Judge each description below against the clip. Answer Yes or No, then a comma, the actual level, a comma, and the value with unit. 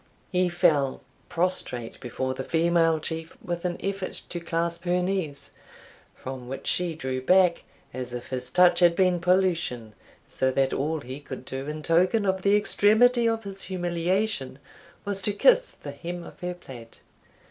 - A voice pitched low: No, medium, 170 Hz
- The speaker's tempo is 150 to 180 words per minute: Yes, average, 165 wpm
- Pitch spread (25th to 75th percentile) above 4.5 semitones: Yes, wide, 5.4 semitones